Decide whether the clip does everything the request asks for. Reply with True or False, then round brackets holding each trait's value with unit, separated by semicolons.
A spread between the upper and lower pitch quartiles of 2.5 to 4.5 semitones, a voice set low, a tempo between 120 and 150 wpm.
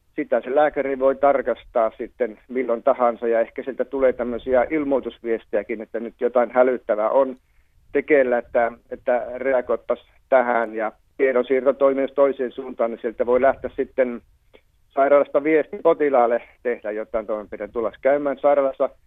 True (2.8 semitones; 125 Hz; 130 wpm)